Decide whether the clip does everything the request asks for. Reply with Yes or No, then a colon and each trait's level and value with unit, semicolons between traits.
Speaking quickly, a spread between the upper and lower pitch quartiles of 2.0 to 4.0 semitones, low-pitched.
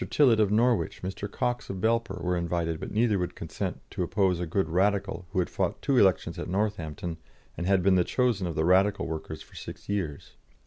Yes: fast, 210 wpm; average, 3.4 semitones; very low, 95 Hz